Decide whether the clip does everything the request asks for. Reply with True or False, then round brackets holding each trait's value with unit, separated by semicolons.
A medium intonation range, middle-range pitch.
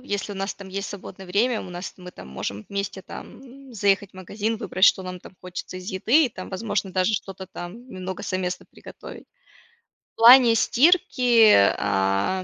False (3.5 semitones; 195 Hz)